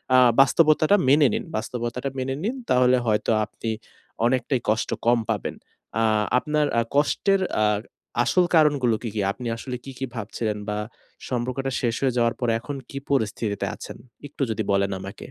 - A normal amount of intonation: Yes, average, 3.5 semitones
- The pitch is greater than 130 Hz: No, low, 125 Hz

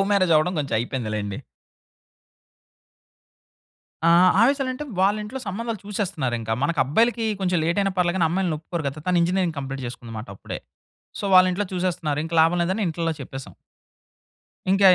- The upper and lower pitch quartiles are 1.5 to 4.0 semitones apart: No, wide, 5.5 semitones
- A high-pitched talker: No, medium, 175 Hz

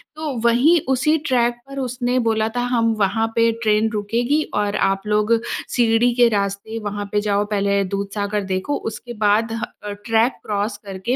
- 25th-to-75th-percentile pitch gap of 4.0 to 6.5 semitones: No, average, 2.9 semitones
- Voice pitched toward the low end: No, high, 220 Hz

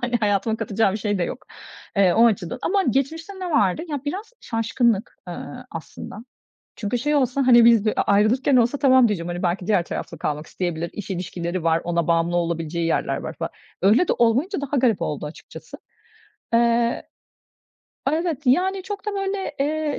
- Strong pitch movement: Yes, wide, 8.0 semitones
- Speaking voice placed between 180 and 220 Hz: No, high, 230 Hz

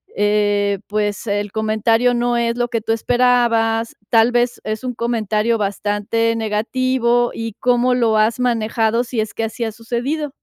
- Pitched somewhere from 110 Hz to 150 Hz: No, high, 230 Hz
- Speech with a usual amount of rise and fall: No, narrow, 2.0 semitones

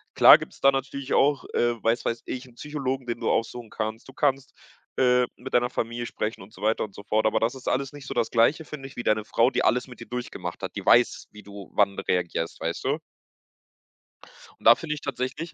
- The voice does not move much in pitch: No, average, 3.2 semitones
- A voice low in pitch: Yes, low, 120 Hz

